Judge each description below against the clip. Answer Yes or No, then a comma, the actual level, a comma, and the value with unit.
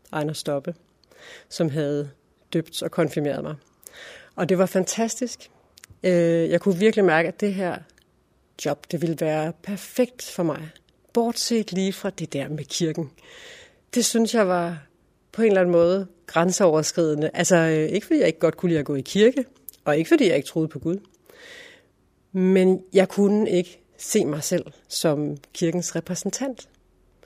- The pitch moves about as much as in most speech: Yes, average, 4.2 semitones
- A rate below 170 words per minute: Yes, average, 160 wpm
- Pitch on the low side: No, medium, 180 Hz